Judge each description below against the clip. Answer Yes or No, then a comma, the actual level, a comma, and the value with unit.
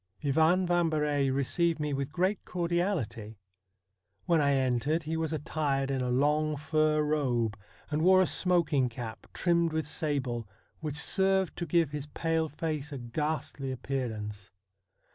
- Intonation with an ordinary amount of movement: Yes, average, 3.3 semitones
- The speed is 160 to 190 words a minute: No, average, 145 wpm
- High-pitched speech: No, medium, 150 Hz